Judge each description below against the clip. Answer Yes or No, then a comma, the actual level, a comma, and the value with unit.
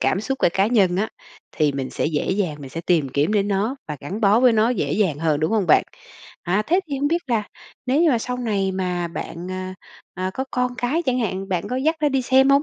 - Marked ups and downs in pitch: Yes, wide, 6.0 semitones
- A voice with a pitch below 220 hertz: Yes, high, 205 Hz